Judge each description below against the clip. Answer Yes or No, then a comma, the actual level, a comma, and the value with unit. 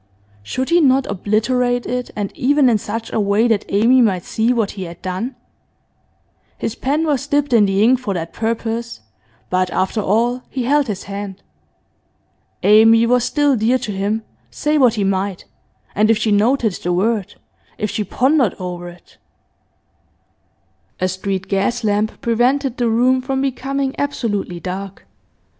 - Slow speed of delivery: No, average, 160 wpm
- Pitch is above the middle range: Yes, high, 225 Hz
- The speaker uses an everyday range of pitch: Yes, average, 4.2 semitones